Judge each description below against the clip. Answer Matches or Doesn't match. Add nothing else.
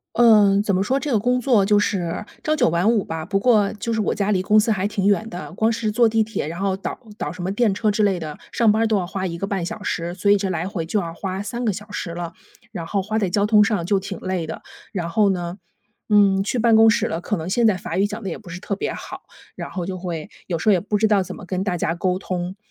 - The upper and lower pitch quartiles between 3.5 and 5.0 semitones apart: Doesn't match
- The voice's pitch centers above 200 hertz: Doesn't match